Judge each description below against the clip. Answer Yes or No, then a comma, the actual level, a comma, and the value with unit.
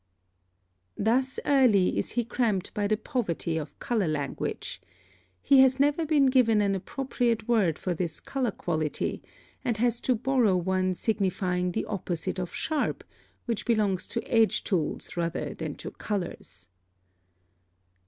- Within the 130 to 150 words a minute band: Yes, average, 145 wpm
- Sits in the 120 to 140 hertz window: No, high, 215 Hz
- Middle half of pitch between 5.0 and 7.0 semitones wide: Yes, average, 5.3 semitones